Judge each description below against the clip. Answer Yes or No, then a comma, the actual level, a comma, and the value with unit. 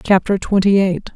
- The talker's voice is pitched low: No, high, 190 Hz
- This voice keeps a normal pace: Yes, average, 155 wpm